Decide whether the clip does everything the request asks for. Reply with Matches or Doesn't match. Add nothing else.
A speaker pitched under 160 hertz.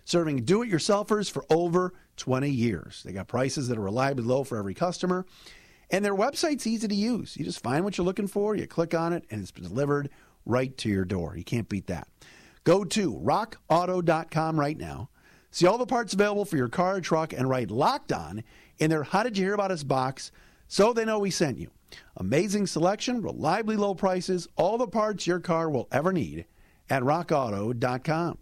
Doesn't match